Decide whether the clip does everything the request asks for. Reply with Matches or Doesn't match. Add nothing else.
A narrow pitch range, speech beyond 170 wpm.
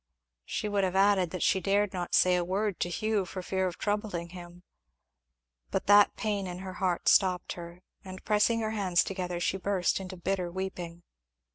Matches